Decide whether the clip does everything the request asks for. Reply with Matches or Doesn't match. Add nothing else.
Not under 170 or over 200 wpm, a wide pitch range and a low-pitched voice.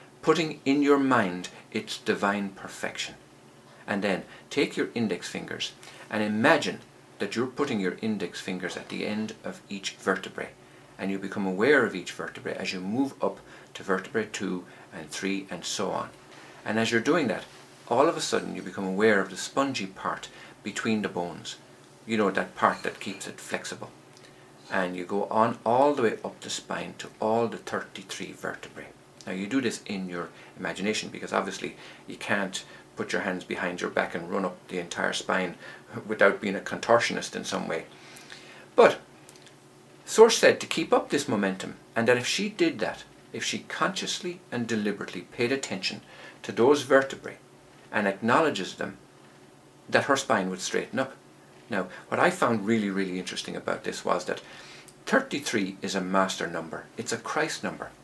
Matches